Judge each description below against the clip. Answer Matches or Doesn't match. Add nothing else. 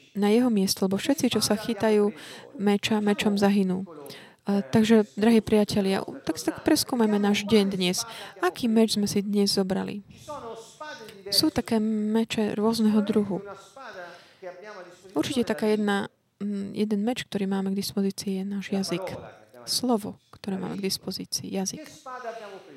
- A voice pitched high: Matches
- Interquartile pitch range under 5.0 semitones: Matches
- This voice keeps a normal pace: Matches